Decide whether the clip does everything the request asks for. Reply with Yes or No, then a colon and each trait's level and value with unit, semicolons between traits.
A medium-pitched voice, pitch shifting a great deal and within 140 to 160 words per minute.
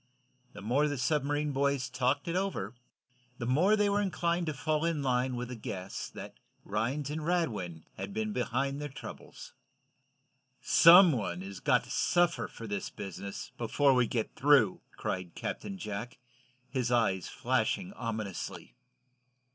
No: low, 130 Hz; wide, 5.9 semitones; average, 150 wpm